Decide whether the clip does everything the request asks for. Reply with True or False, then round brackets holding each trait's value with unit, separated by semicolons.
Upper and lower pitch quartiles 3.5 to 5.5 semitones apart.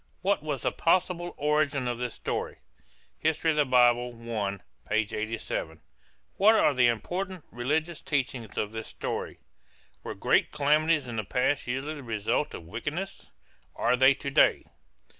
True (4.8 semitones)